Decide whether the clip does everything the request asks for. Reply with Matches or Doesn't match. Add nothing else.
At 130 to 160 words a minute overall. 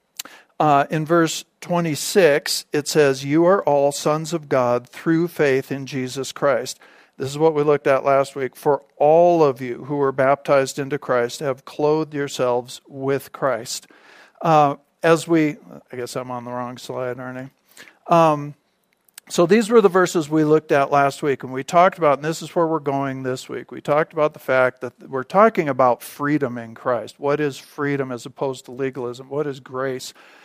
Doesn't match